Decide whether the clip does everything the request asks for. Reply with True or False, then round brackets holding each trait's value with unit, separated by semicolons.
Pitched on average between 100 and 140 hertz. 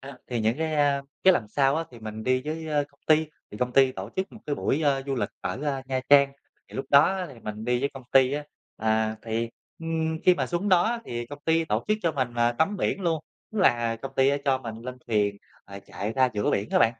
True (135 Hz)